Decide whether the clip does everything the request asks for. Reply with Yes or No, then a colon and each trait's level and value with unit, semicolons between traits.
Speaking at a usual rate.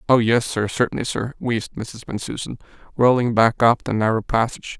Yes: average, 165 wpm